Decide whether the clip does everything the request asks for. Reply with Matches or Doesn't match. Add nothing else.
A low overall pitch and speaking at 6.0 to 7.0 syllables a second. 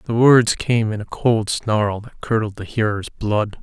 Doesn't match